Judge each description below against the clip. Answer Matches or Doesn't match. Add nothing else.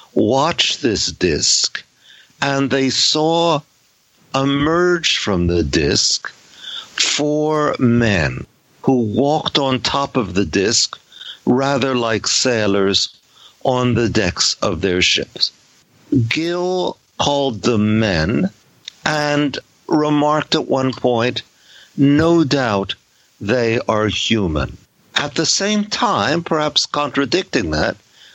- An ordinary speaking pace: Doesn't match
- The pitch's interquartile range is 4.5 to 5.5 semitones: Matches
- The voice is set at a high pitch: Doesn't match